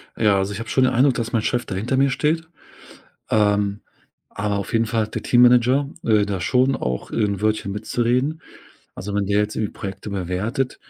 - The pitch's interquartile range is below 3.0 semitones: No, average, 3.6 semitones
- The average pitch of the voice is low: Yes, low, 110 Hz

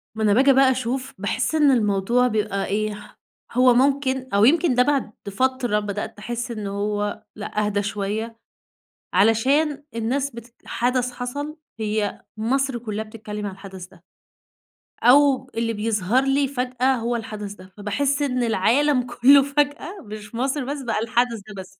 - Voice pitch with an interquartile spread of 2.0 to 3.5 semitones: No, average, 4.1 semitones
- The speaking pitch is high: Yes, high, 235 Hz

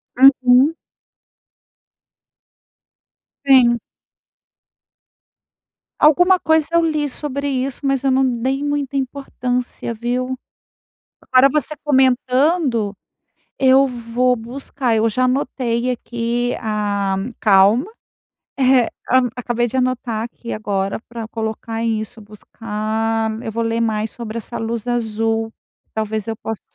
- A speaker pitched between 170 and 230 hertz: No, high, 240 Hz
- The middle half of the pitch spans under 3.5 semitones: Yes, average, 3.0 semitones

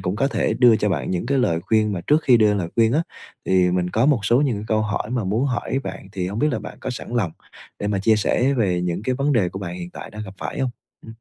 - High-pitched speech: No, low, 105 Hz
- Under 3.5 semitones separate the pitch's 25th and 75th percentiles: No, average, 4.8 semitones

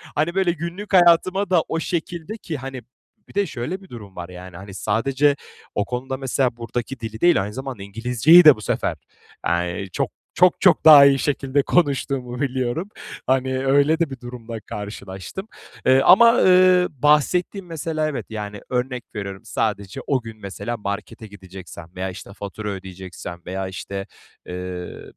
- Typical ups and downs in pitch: No, wide, 7.6 semitones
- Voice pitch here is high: No, low, 125 Hz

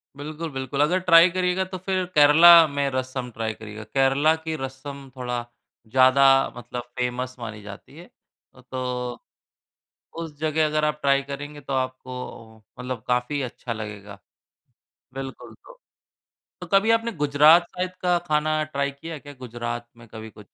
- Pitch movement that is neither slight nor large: Yes, average, 3.9 semitones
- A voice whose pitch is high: No, low, 135 Hz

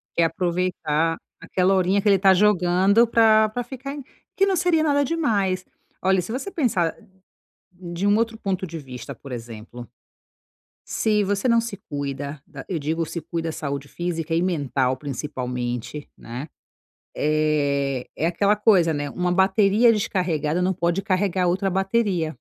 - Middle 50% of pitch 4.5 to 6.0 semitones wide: Yes, average, 5.1 semitones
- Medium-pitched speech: Yes, medium, 180 Hz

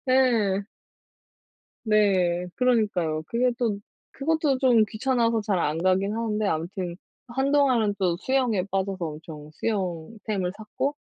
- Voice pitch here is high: Yes, high, 210 Hz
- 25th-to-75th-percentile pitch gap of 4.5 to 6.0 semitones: Yes, average, 5.1 semitones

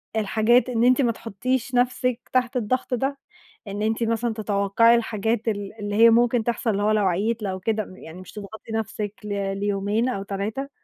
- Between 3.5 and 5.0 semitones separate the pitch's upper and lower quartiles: No, average, 2.8 semitones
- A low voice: No, high, 220 Hz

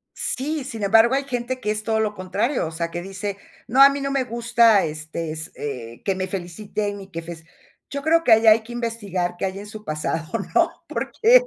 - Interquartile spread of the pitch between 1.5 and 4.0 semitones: No, wide, 5.4 semitones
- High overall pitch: Yes, high, 210 Hz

